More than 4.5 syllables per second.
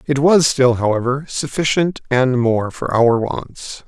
No: 3.9 syllables/s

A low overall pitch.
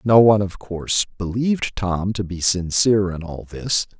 Yes: low, 100 Hz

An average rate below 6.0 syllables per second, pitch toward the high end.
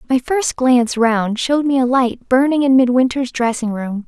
Yes: 4.9 syllables/s; very high, 250 Hz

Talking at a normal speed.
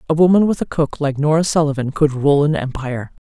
No: fast, 220 wpm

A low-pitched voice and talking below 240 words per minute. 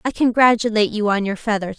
No: high, 220 Hz; average, 200 wpm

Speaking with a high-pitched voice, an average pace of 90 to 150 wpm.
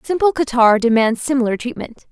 Yes: very high, 250 Hz; average, 140 wpm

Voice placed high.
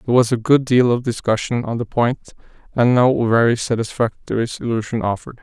No: low, 120 Hz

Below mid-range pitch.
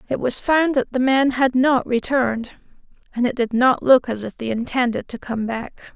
No: very high, 250 Hz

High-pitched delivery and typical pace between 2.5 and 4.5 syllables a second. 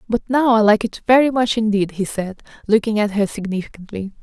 No: high, 215 Hz; 5.8 syllables/s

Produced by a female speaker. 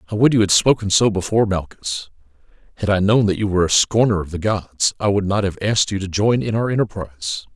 No: male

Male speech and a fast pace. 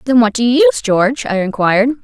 No: female; fast, 235 wpm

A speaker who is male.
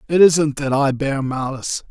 Yes: male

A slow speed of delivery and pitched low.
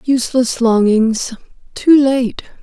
No: slow, 90 wpm; high, 245 Hz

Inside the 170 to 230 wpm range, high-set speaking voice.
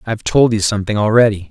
No: average, 200 wpm; low, 105 Hz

